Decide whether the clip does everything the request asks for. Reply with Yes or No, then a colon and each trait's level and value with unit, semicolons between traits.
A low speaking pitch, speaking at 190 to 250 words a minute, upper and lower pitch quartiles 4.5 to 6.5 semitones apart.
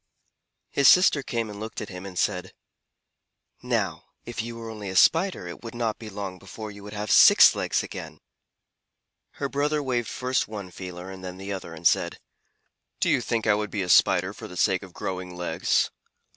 No: low, 105 Hz; average, 200 wpm; average, 3.8 semitones